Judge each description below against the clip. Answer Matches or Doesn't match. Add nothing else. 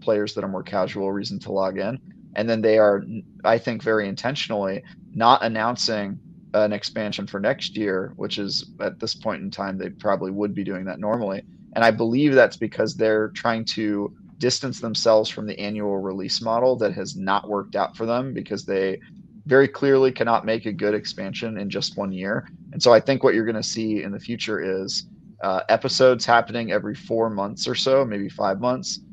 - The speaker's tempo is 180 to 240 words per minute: Matches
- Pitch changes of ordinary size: Matches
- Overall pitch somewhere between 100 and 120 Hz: Matches